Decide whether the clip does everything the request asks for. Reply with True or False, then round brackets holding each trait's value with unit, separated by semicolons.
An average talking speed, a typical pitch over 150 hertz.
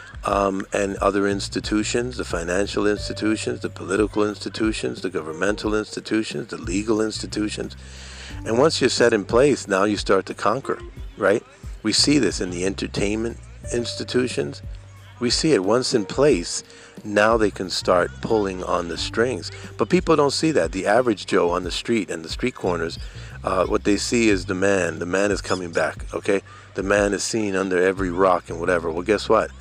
False (180 wpm; 100 Hz)